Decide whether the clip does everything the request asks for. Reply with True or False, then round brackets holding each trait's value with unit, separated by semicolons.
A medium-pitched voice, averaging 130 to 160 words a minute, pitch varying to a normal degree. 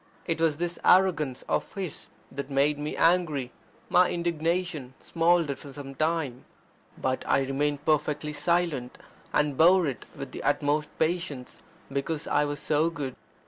True (150 Hz; 145 wpm; 3.2 semitones)